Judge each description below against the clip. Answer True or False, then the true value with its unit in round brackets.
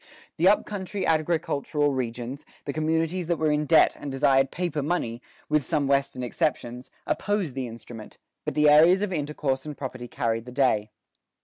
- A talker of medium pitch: True (145 Hz)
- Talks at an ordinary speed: True (170 wpm)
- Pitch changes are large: False (3.9 semitones)